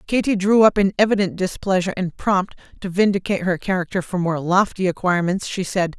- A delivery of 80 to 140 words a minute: No, average, 180 wpm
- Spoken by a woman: Yes, female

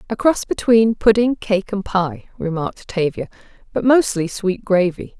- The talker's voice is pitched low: No, high, 200 Hz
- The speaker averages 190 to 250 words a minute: No, average, 150 wpm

